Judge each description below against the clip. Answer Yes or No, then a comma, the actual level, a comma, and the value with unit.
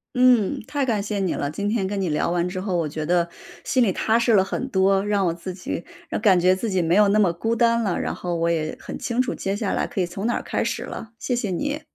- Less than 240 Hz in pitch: Yes, high, 195 Hz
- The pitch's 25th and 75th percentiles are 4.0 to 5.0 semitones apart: Yes, average, 4.3 semitones